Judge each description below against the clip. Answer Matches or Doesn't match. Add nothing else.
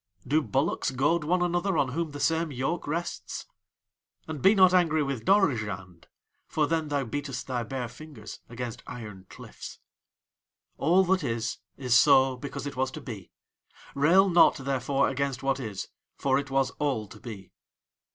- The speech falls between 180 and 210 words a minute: Doesn't match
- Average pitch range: Matches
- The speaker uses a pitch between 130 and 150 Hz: Matches